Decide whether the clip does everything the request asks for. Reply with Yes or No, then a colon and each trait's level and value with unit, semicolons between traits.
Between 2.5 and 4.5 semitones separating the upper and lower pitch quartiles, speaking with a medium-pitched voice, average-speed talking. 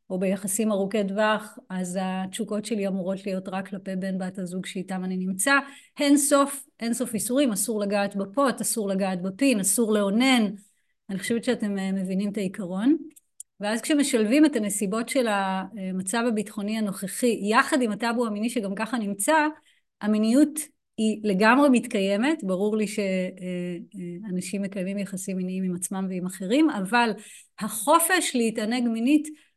No: average, 4.2 semitones; high, 215 Hz; average, 140 wpm